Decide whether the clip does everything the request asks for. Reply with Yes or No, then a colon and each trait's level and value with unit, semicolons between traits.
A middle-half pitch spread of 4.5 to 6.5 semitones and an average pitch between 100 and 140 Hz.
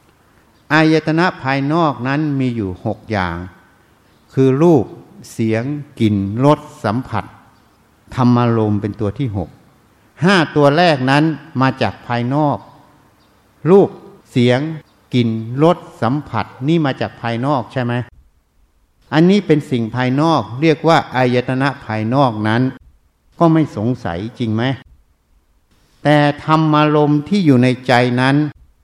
Yes: wide, 5.6 semitones; low, 125 Hz